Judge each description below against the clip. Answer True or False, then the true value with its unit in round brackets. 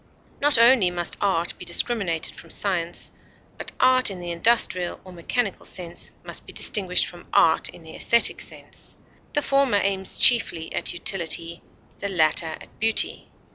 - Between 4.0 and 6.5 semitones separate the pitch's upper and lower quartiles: True (5.1 semitones)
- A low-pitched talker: False (185 Hz)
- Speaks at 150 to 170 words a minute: True (155 wpm)